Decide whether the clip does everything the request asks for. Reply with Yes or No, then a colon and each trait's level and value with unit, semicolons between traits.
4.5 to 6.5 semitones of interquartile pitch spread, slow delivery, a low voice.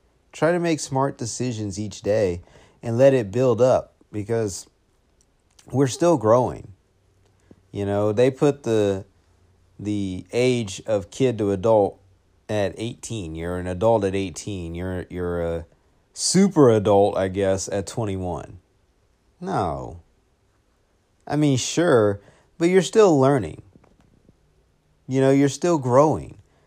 Yes: average, 5.3 semitones; slow, 125 wpm; low, 105 Hz